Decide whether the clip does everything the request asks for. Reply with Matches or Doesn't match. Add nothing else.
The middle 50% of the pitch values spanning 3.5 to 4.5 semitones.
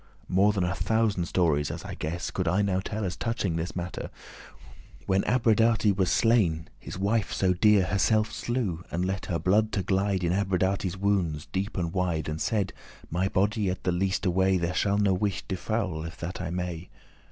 Doesn't match